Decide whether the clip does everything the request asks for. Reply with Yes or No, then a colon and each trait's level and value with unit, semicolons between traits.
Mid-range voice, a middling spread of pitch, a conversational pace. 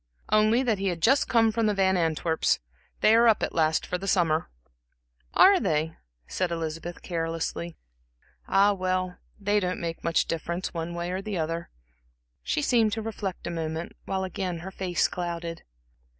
Yes: medium, 180 Hz; average, 3.6 semitones; average, 170 wpm